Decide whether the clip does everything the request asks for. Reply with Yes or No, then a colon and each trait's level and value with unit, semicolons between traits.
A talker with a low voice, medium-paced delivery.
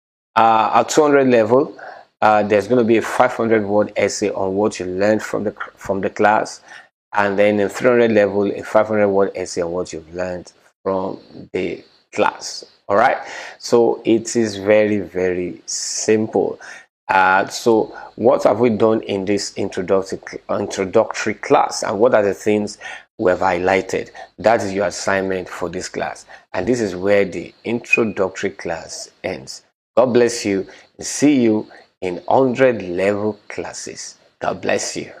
Yes: low, 105 Hz; average, 160 wpm